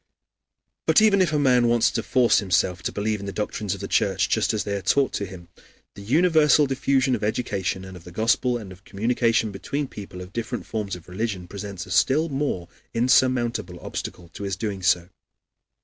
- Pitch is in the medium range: No, low, 105 Hz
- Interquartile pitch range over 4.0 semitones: Yes, average, 5.1 semitones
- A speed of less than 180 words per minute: No, average, 200 wpm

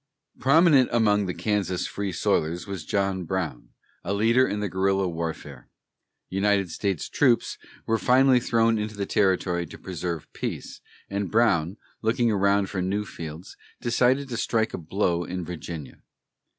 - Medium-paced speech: Yes, average, 150 wpm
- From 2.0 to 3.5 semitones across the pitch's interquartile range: No, average, 4.2 semitones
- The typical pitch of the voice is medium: No, low, 100 Hz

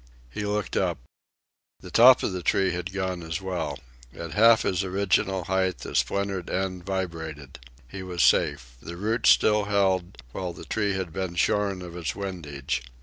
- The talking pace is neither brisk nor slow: Yes, average, 170 wpm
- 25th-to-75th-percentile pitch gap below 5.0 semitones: Yes, narrow, 2.5 semitones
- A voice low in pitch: Yes, very low, 95 Hz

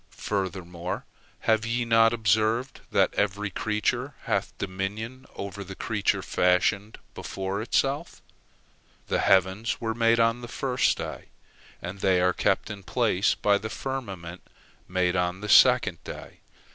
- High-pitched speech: No, low, 105 Hz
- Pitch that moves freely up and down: No, average, 3.3 semitones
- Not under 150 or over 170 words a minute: No, slow, 135 wpm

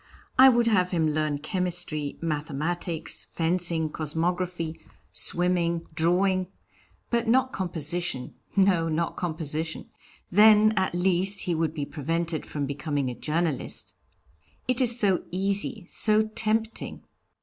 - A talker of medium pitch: Yes, medium, 175 Hz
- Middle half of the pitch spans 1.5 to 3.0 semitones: No, average, 3.7 semitones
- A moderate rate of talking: No, slow, 115 wpm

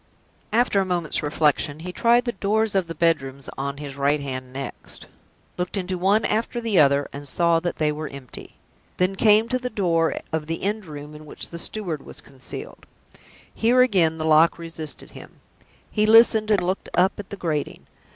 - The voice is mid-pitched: Yes, medium, 170 Hz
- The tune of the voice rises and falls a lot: Yes, wide, 5.7 semitones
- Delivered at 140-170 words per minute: No, average, 190 wpm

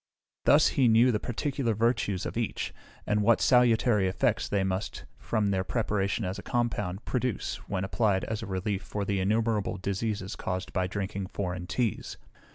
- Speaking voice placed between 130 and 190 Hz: No, low, 105 Hz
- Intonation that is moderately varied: Yes, average, 3.3 semitones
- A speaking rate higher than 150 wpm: Yes, average, 165 wpm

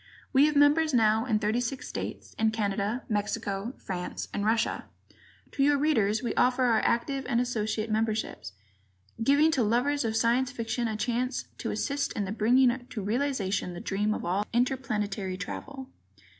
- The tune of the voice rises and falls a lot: No, average, 3.7 semitones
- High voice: Yes, high, 230 Hz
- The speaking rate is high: No, average, 165 wpm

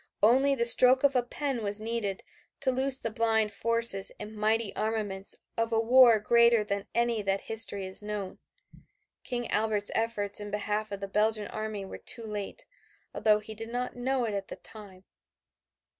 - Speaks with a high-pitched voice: Yes, high, 220 Hz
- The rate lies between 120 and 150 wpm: No, average, 175 wpm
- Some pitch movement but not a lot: No, narrow, 2.2 semitones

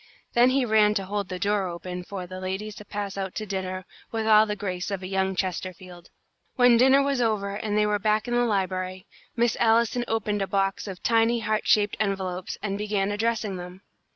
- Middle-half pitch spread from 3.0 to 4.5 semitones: No, narrow, 2.6 semitones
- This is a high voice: Yes, high, 205 Hz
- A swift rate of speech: Yes, fast, 210 wpm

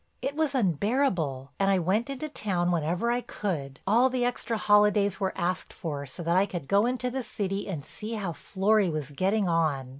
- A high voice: Yes, high, 195 Hz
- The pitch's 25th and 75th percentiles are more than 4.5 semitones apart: Yes, average, 5.2 semitones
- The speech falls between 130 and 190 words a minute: No, average, 200 wpm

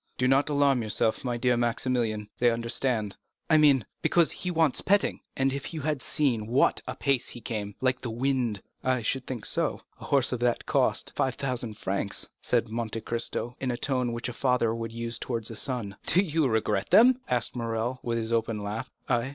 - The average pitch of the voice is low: Yes, low, 120 Hz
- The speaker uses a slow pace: No, average, 185 wpm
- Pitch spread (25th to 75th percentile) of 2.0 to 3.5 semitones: Yes, average, 2.7 semitones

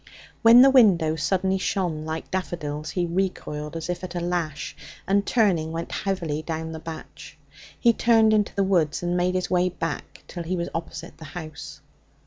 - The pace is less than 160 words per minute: No, average, 180 wpm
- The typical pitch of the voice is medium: Yes, medium, 175 Hz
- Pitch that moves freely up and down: No, average, 3.1 semitones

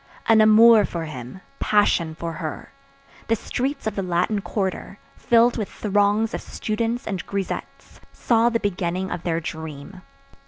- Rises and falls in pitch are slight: No, average, 4.7 semitones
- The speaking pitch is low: No, high, 200 Hz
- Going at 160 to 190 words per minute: No, average, 150 wpm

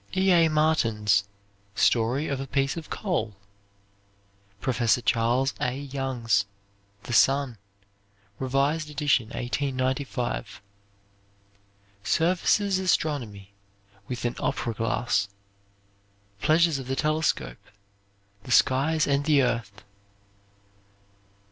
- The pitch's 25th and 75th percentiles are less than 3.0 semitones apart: No, average, 4.6 semitones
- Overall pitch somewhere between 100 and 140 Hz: Yes, low, 135 Hz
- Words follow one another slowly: Yes, slow, 90 wpm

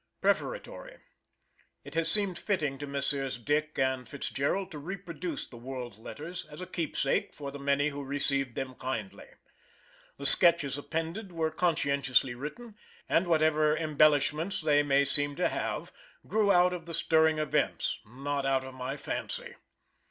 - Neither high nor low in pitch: Yes, medium, 150 Hz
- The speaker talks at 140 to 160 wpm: Yes, average, 150 wpm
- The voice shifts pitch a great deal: No, average, 3.5 semitones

